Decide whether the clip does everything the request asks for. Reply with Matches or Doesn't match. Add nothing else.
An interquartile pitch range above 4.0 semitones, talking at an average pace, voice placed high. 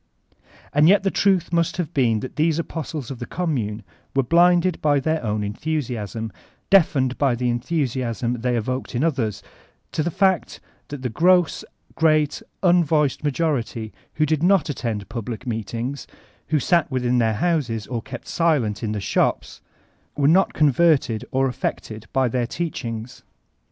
Doesn't match